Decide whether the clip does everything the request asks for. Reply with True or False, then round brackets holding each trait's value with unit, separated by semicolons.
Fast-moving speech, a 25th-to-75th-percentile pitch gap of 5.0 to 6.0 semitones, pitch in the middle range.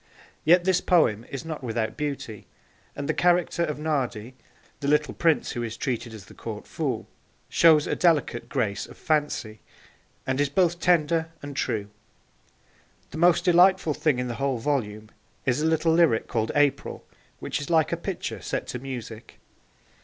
False (170 wpm; 5.6 semitones; 145 Hz)